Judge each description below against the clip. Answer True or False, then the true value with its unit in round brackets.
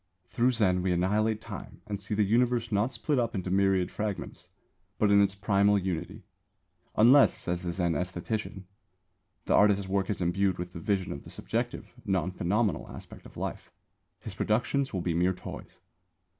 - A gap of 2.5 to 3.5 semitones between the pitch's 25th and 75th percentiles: True (2.8 semitones)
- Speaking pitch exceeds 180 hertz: False (100 Hz)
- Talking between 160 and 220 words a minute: True (170 wpm)